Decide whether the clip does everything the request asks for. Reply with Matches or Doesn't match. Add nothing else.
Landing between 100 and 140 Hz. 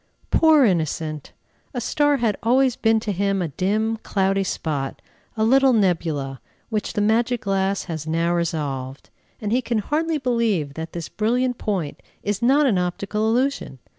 Doesn't match